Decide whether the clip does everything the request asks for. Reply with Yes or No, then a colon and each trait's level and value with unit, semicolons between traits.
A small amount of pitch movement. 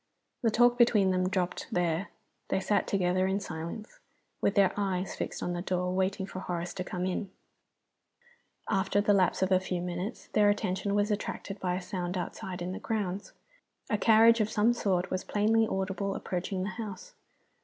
Yes: narrow, 2.2 semitones